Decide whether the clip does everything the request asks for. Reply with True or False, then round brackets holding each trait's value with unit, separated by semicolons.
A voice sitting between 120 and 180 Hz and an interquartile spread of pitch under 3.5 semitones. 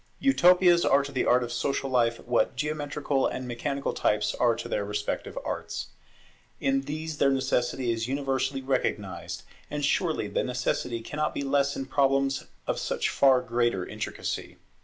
True (135 Hz; 2.6 semitones)